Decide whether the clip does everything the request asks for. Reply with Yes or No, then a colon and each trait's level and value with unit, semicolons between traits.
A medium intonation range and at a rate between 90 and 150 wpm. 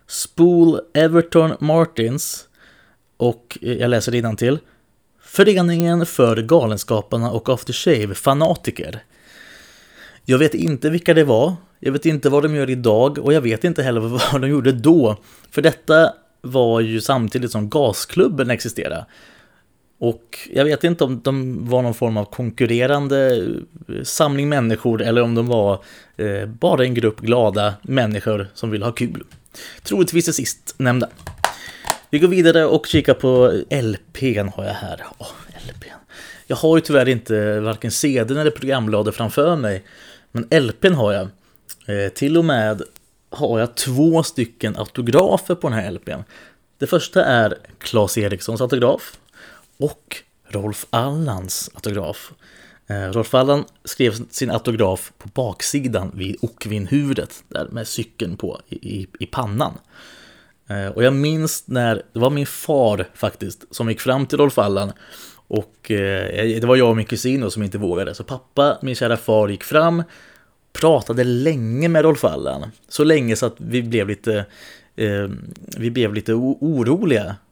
Yes: average, 4.8 semitones; average, 145 wpm